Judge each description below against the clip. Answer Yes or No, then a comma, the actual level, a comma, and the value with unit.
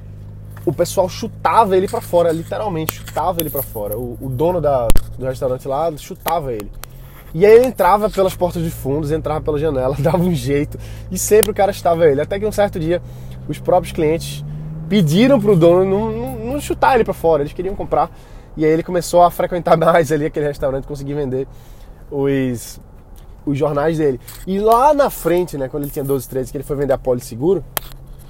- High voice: No, medium, 155 Hz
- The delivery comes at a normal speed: No, fast, 195 wpm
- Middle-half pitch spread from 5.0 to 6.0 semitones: Yes, average, 5.3 semitones